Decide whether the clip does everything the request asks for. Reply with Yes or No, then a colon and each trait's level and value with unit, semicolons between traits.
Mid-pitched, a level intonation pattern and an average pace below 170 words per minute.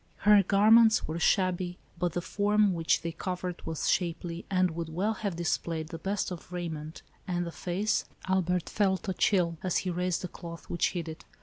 No: medium, 180 Hz; narrow, 2.3 semitones; average, 195 wpm